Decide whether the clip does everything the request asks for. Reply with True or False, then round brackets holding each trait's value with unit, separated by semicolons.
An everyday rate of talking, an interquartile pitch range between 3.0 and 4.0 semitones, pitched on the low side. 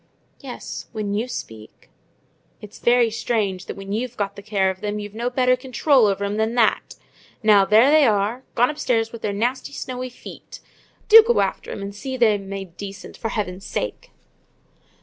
False (175 wpm; 3.7 semitones; 220 Hz)